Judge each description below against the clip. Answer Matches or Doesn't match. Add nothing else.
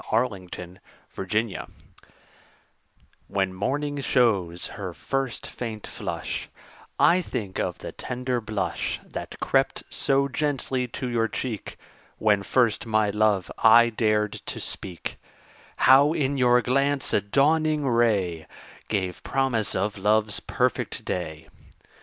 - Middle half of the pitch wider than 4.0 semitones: Matches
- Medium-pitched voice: Doesn't match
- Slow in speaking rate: Matches